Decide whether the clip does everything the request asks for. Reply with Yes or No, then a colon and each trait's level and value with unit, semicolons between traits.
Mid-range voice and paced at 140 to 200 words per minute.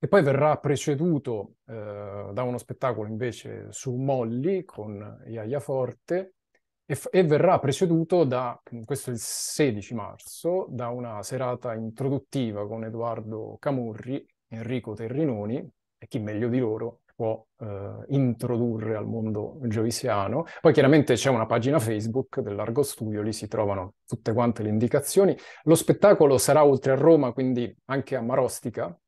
No: low, 125 Hz; average, 145 wpm